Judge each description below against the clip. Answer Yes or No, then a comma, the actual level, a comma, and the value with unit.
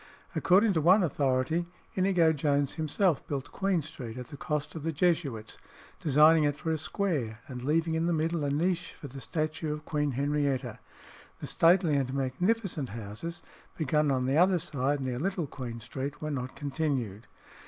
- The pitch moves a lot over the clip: No, average, 3.8 semitones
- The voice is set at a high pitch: No, medium, 150 Hz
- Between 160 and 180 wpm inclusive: Yes, average, 175 wpm